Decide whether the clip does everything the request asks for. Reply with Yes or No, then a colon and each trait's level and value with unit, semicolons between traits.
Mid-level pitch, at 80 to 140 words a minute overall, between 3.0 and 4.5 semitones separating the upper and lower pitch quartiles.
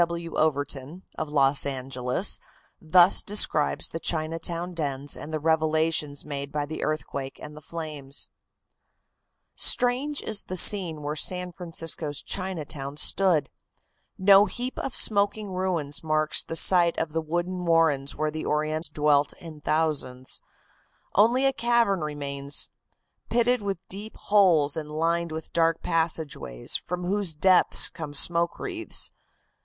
Yes: medium, 160 Hz; slow, 135 wpm; average, 3.7 semitones